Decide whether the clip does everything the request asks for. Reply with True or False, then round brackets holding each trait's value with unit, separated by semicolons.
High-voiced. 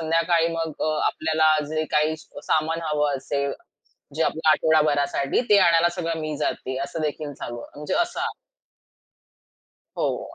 False (155 Hz)